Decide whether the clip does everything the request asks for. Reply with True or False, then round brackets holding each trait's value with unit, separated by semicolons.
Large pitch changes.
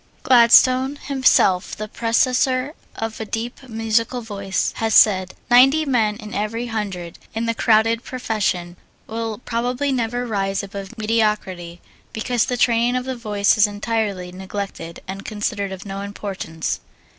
False (3.3 semitones)